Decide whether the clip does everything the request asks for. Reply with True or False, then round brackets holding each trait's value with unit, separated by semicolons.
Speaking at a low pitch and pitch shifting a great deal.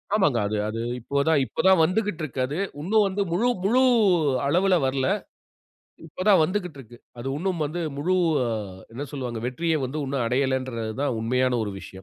False (145 Hz; 6.3 semitones)